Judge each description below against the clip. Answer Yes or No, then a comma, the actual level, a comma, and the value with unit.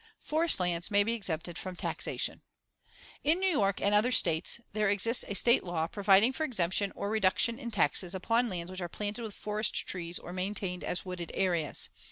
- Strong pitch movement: No, average, 4.1 semitones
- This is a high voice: Yes, high, 200 Hz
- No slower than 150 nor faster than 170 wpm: No, average, 190 wpm